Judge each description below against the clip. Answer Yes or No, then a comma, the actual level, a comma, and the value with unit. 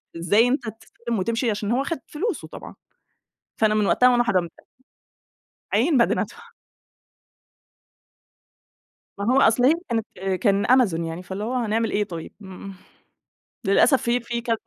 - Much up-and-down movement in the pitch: No, average, 3.6 semitones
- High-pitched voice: Yes, high, 225 Hz